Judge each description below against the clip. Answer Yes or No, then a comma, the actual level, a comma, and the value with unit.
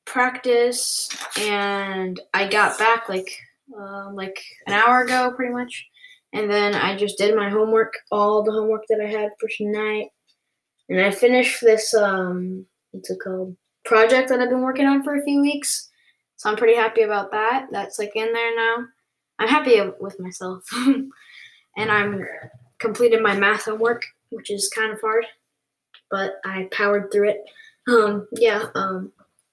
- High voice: Yes, high, 215 Hz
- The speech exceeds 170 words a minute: No, average, 165 wpm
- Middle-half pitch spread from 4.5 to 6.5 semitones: No, average, 2.9 semitones